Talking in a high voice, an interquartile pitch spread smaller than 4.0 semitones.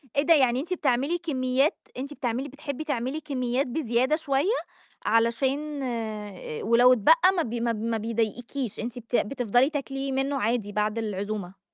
Yes: very high, 255 Hz; average, 3.5 semitones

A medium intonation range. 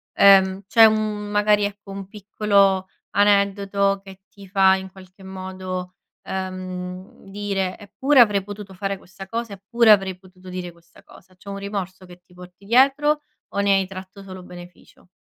No: narrow, 1.6 semitones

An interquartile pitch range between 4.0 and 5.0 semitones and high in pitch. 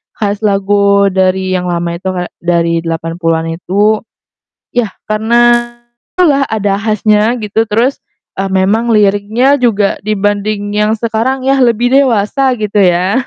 No: average, 3.3 semitones; high, 210 Hz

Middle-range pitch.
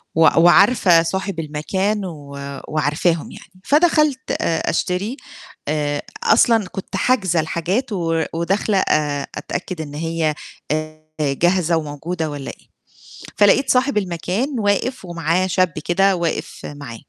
Yes: medium, 175 Hz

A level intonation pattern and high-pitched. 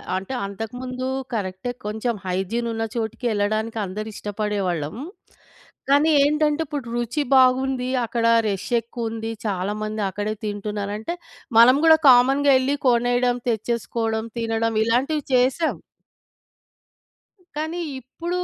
No: average, 3.5 semitones; high, 230 Hz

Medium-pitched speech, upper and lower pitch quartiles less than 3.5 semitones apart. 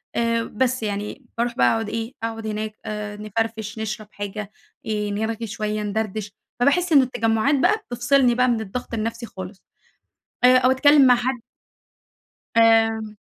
No: high, 225 Hz; narrow, 2.5 semitones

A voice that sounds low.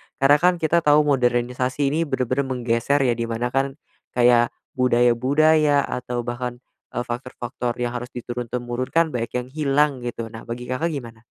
Yes: low, 125 Hz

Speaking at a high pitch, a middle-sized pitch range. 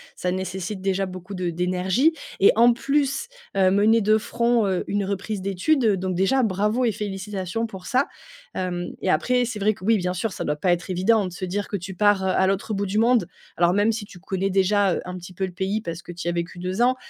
Yes: high, 195 Hz; average, 3.0 semitones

